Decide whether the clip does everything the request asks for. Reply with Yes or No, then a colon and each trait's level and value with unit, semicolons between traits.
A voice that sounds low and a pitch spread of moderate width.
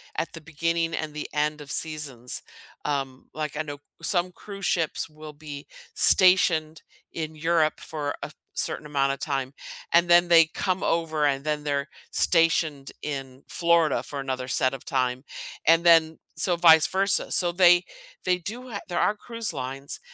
No: medium, 155 Hz; average, 3.1 semitones